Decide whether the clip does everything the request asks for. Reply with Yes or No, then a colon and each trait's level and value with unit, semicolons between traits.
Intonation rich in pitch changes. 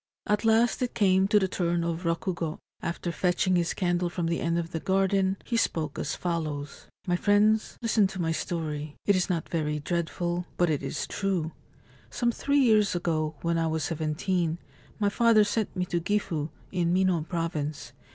No: average, 3.0 semitones